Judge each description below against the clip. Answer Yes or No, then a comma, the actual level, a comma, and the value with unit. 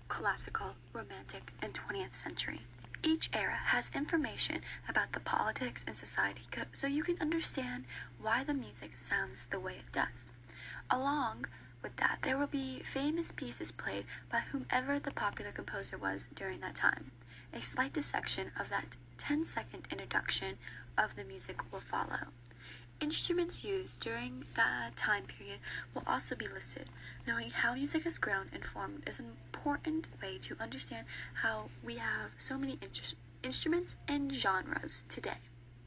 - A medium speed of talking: Yes, average, 150 wpm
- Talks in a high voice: Yes, very high, 270 Hz